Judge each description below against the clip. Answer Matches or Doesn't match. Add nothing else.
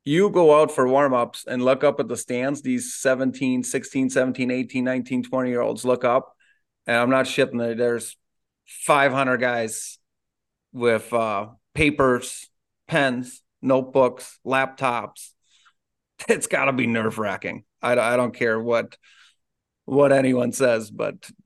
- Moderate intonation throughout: Doesn't match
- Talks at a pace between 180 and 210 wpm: Doesn't match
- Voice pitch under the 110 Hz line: Doesn't match